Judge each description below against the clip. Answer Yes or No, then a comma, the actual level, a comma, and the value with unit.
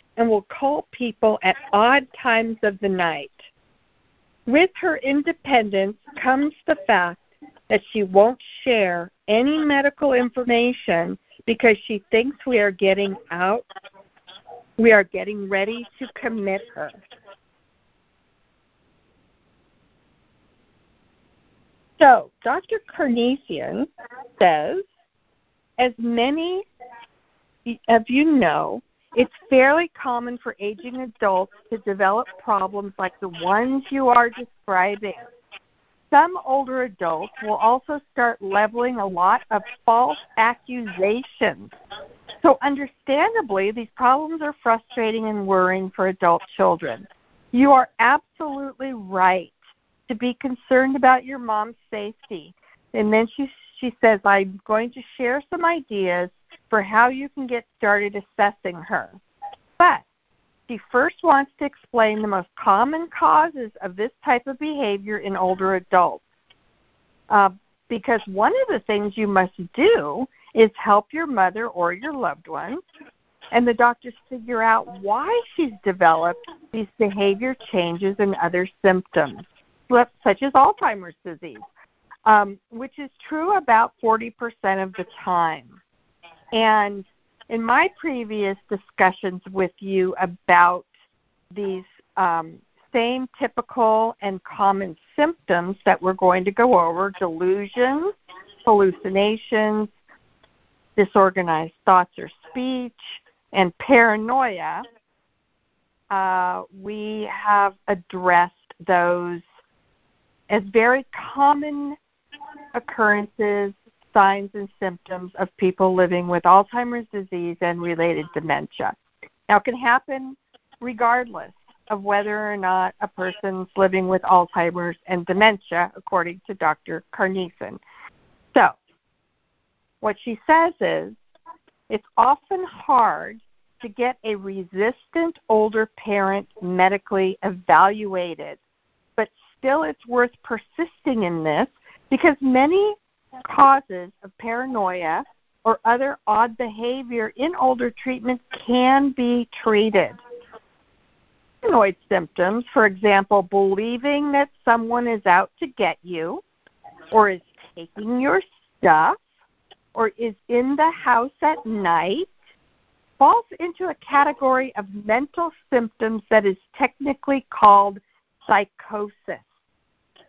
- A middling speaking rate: No, slow, 115 wpm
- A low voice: No, high, 220 Hz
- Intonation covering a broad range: No, average, 4.9 semitones